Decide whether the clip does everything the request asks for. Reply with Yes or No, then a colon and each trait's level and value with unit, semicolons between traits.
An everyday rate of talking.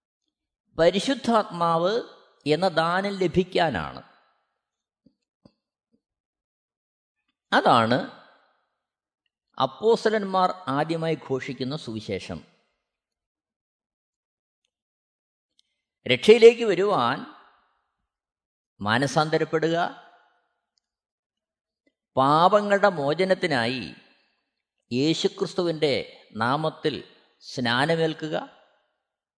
No: slow, 35 wpm